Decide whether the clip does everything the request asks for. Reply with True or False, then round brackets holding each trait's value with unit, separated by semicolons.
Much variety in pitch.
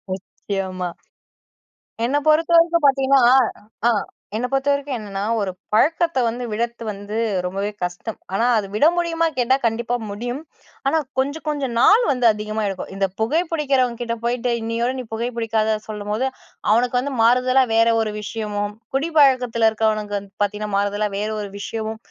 False (4.2 semitones)